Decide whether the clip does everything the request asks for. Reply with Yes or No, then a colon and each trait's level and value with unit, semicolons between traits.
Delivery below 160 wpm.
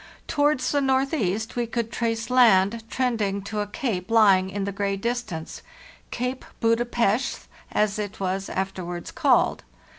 Yes: average, 150 wpm